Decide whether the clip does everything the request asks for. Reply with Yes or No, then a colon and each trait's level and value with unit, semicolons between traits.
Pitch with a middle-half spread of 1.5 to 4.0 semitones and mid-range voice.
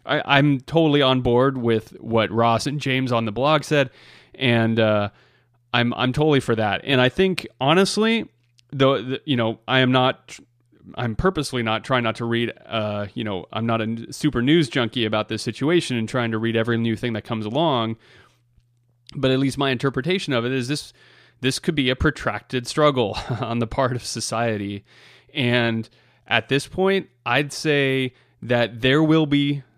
No: average, 3.4 semitones; low, 125 Hz